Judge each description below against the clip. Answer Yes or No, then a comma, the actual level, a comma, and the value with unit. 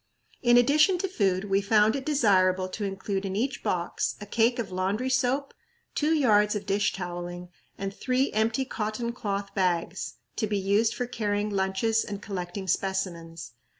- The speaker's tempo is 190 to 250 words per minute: No, average, 165 wpm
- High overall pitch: Yes, high, 205 Hz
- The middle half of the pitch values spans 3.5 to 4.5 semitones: Yes, average, 3.8 semitones